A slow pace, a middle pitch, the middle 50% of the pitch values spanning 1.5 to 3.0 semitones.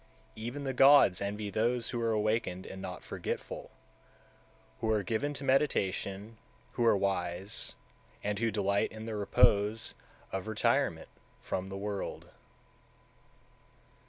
No: slow, 130 wpm; low, 105 Hz; average, 2.7 semitones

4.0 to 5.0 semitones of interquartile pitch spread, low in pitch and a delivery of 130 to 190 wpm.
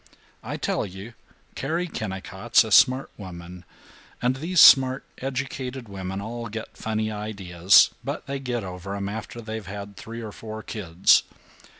Yes: average, 4.4 semitones; low, 110 Hz; average, 150 wpm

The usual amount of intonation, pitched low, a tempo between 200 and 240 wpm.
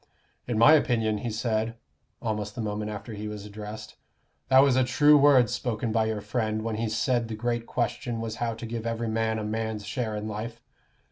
No: narrow, 1.8 semitones; low, 110 Hz; fast, 205 wpm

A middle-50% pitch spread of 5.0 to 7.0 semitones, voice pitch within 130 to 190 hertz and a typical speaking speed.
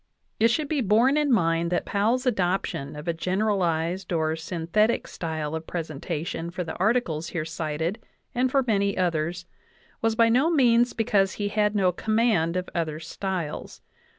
Yes: average, 5.3 semitones; medium, 185 Hz; average, 165 wpm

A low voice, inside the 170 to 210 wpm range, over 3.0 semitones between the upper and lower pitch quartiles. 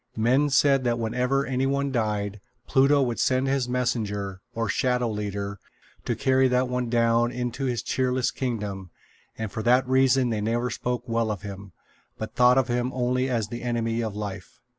No: low, 120 Hz; average, 180 wpm; average, 2.7 semitones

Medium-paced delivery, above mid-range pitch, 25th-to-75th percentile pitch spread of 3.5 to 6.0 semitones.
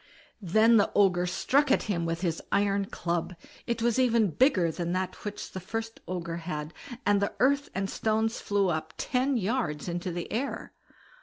Yes: average, 175 wpm; high, 195 Hz; average, 4.5 semitones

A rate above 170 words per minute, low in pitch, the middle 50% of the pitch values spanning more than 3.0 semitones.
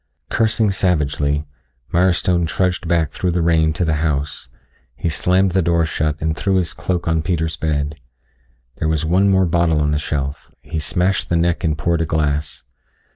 No: average, 180 wpm; very low, 80 Hz; narrow, 2.6 semitones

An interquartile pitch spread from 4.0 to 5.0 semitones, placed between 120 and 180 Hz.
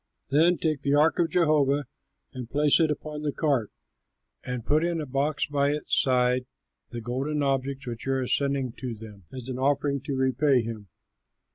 No: average, 2.9 semitones; medium, 140 Hz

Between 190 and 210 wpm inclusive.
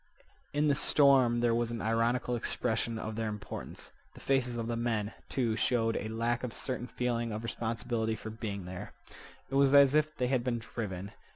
Yes: average, 195 wpm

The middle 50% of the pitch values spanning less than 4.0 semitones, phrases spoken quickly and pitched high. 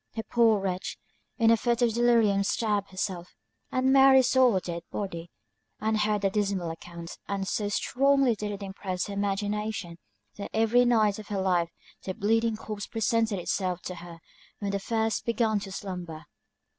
No: average, 2.9 semitones; average, 170 wpm; high, 205 Hz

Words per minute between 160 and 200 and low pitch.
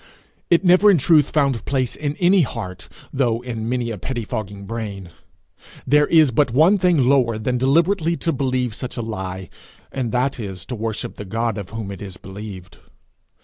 Yes: average, 180 wpm; low, 120 Hz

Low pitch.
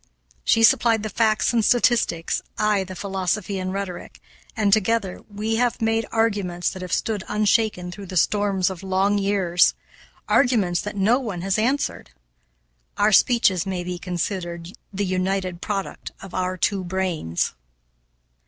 No: high, 195 Hz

